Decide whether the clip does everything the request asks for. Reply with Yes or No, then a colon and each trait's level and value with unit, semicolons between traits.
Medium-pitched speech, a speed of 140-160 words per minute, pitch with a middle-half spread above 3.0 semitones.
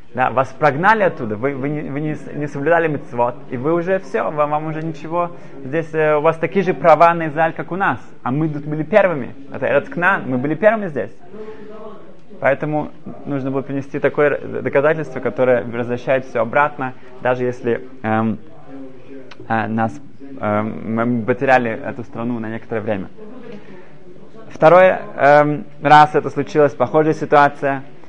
Yes: medium, 145 Hz; average, 155 wpm; average, 4.1 semitones